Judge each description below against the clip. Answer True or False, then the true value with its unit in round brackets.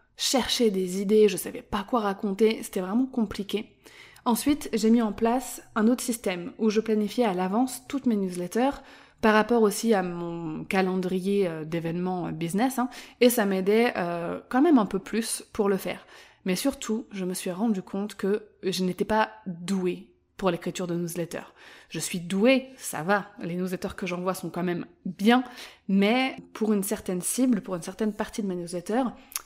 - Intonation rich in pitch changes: False (4.2 semitones)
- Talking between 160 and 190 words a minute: True (180 wpm)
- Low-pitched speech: False (210 Hz)